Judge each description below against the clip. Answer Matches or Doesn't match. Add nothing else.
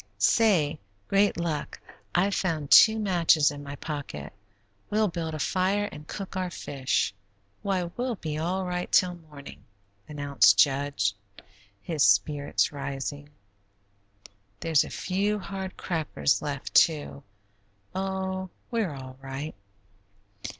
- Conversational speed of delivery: Doesn't match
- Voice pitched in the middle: Matches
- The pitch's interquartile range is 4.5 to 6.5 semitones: Matches